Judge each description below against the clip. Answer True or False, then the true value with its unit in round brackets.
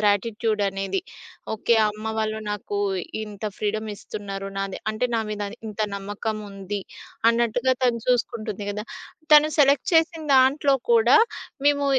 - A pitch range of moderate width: True (3.2 semitones)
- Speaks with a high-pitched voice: True (215 Hz)